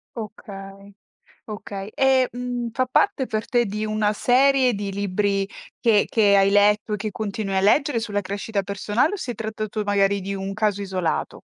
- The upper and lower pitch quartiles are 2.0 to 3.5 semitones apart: Yes, average, 2.8 semitones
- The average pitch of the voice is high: Yes, high, 210 Hz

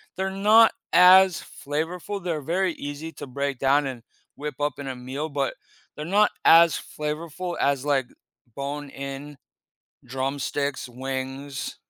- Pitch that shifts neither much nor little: Yes, average, 3.7 semitones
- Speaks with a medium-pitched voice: Yes, medium, 145 Hz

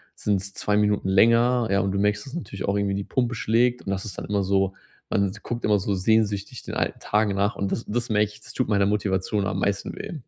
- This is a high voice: No, low, 105 Hz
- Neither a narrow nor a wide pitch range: No, narrow, 2.0 semitones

